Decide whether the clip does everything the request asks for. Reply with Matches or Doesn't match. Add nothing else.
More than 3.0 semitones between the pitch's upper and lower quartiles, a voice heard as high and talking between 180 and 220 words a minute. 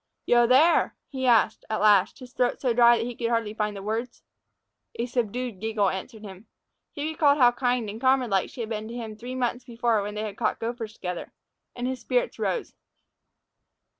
Doesn't match